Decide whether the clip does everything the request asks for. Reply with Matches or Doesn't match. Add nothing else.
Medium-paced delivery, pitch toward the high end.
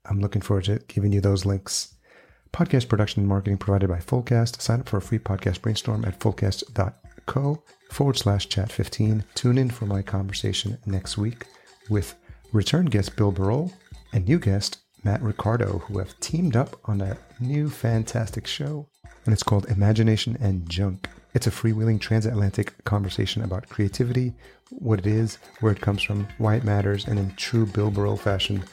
Doesn't match